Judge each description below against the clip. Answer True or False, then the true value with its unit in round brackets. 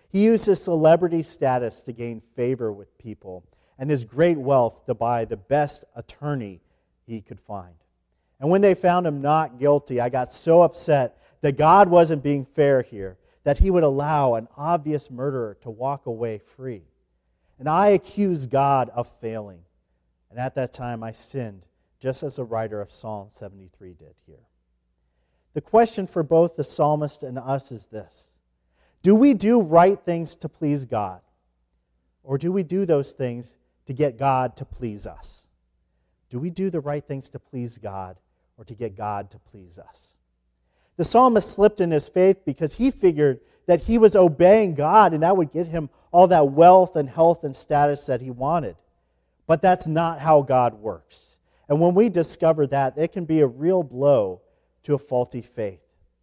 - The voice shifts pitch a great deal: True (7.8 semitones)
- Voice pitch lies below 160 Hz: True (135 Hz)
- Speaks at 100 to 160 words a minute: False (180 wpm)